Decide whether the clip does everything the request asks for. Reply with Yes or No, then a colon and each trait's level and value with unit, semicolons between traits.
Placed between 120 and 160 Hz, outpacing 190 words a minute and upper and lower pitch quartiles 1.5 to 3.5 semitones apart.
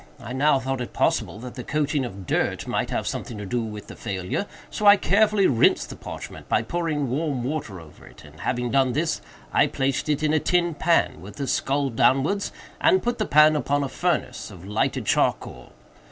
No: low, 135 Hz; fast, 205 wpm; average, 4.7 semitones